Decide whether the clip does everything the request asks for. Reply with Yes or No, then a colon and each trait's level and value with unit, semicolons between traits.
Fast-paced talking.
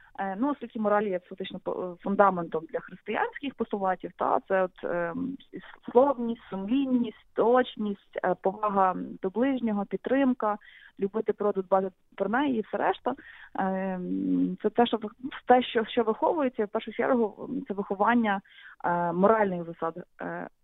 No: average, 135 wpm